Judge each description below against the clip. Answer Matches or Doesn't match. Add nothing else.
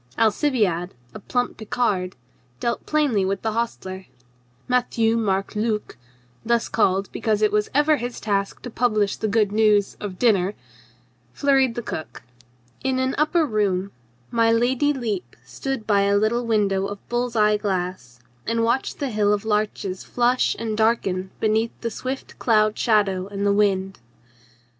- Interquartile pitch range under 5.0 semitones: Matches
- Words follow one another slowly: Doesn't match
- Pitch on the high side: Matches